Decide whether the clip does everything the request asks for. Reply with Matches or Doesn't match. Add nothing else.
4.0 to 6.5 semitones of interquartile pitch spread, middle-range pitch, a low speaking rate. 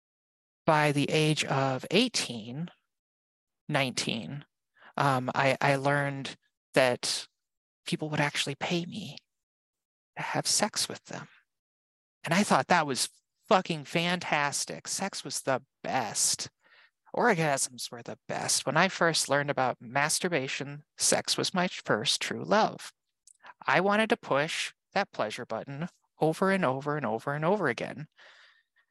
Matches